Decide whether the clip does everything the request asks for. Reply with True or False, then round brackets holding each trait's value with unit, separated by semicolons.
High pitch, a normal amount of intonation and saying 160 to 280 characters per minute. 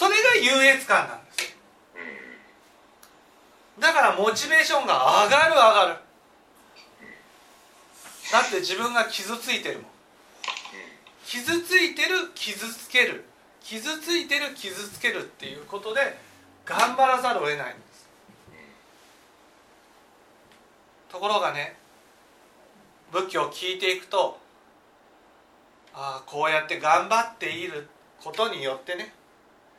False (230 Hz; 7.7 semitones; 225 characters per minute)